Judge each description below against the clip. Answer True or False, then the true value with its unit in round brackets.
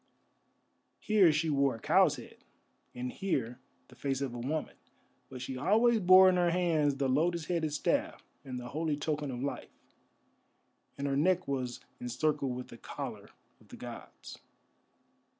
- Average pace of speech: True (160 wpm)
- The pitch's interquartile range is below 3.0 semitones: False (4.7 semitones)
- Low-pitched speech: False (145 Hz)